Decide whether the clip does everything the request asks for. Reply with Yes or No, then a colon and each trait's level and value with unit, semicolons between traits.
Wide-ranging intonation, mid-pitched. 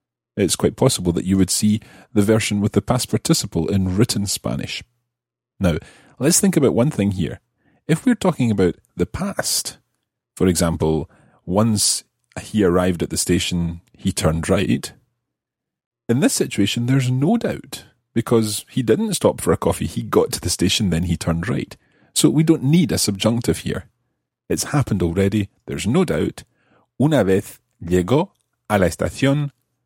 No: wide, 5.9 semitones; low, 105 Hz